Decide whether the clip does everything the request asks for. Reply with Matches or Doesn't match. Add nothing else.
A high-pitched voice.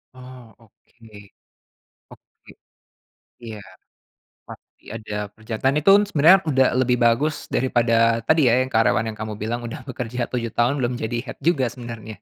Doesn't match